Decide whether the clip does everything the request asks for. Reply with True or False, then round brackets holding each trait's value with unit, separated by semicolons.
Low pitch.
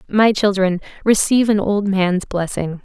False (195 Hz)